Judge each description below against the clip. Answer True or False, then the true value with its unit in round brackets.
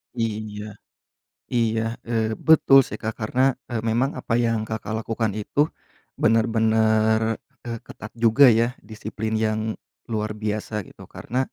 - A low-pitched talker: True (110 Hz)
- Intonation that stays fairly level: True (1.2 semitones)